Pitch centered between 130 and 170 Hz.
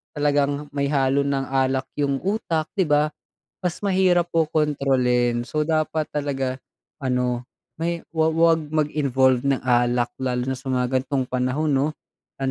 Yes: medium, 140 Hz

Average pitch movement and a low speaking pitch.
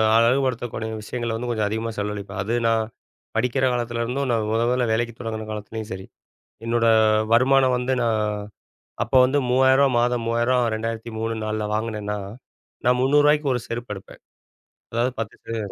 No: narrow, 2.2 semitones; low, 115 Hz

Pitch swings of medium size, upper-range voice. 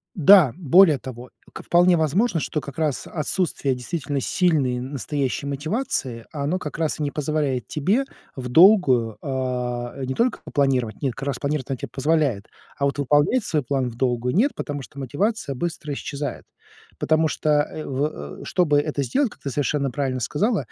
No: average, 3.6 semitones; medium, 145 Hz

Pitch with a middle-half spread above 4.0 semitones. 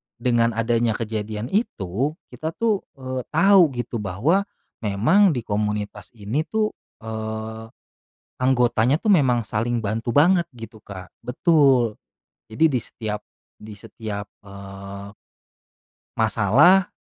Yes: wide, 5.4 semitones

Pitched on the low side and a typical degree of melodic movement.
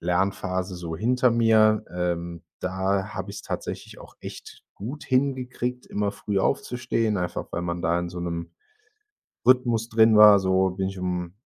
Yes: very low, 95 Hz; average, 4.3 semitones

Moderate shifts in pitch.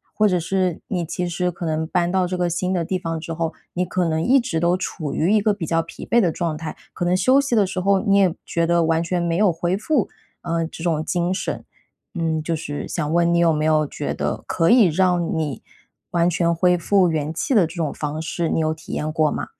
No: narrow, 2.3 semitones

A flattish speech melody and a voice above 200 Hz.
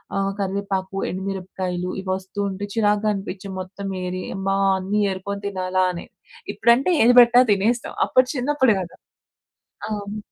No: narrow, 2.2 semitones; high, 195 Hz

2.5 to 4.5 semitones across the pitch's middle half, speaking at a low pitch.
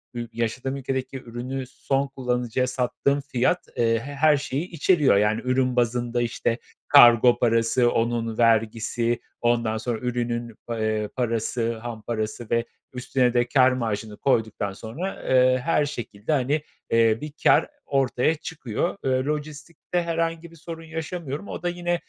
Yes: average, 3.6 semitones; low, 125 Hz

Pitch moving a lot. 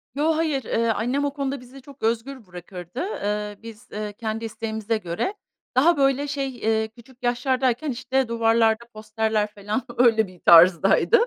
No: average, 3.8 semitones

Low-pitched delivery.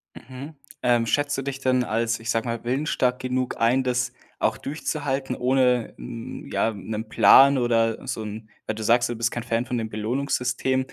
Yes: low, 125 Hz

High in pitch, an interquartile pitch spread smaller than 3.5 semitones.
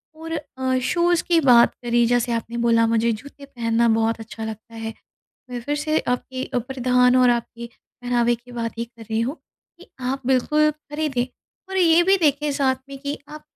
No: very high, 250 Hz; average, 3.9 semitones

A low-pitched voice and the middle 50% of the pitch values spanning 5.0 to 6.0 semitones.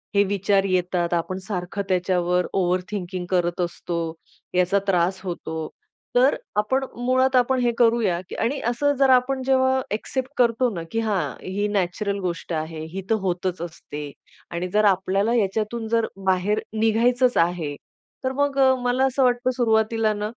No: high, 205 Hz; average, 5.3 semitones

